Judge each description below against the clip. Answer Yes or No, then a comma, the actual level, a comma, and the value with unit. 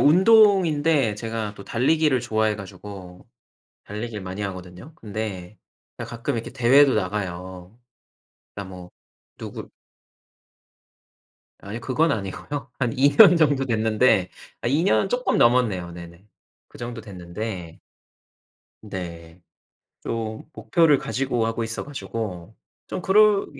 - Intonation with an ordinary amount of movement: No, wide, 6.2 semitones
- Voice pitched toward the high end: No, low, 110 Hz